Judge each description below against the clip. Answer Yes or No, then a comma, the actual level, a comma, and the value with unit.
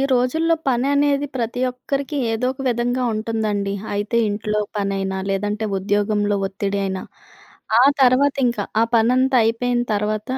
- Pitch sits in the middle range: No, high, 225 Hz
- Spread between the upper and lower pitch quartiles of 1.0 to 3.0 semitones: No, average, 3.6 semitones